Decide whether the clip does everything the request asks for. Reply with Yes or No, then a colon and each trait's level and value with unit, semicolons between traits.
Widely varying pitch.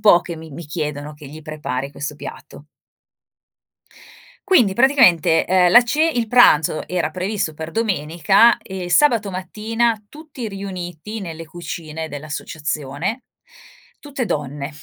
Yes: wide, 6.2 semitones